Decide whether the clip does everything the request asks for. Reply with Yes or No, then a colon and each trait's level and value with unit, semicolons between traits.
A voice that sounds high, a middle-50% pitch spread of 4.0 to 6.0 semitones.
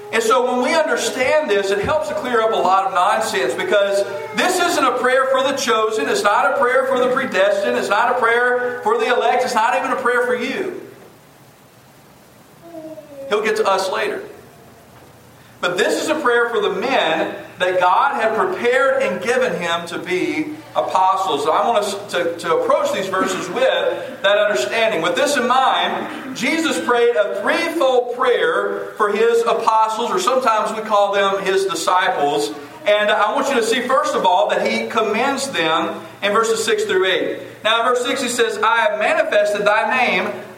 Yes: high, 230 Hz; average, 4.8 semitones